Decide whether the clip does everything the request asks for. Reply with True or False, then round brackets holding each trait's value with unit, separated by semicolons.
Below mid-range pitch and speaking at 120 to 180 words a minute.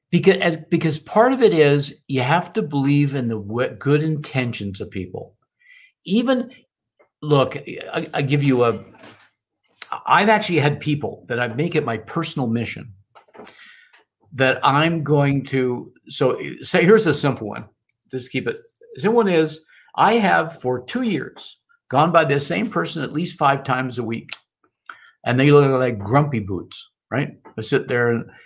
False (145 Hz; 165 wpm)